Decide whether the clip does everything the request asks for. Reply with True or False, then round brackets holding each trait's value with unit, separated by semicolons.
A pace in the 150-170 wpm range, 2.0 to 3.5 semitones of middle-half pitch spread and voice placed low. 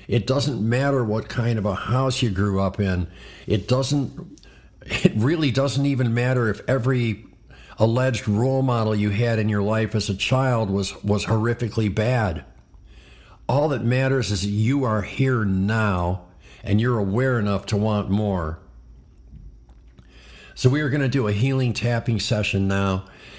False (160 wpm; 4.5 semitones; 110 Hz)